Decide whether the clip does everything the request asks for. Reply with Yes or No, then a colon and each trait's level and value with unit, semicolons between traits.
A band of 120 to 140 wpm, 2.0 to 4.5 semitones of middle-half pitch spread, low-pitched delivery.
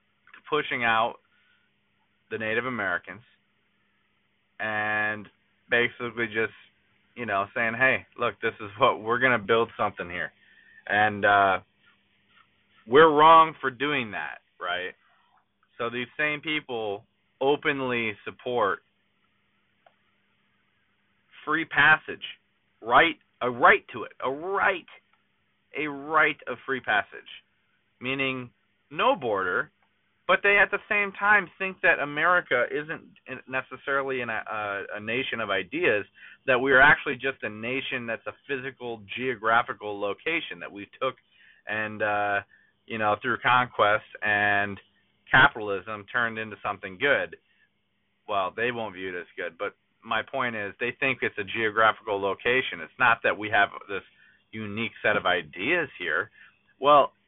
Yes: slow, 135 wpm; average, 4.2 semitones; low, 120 Hz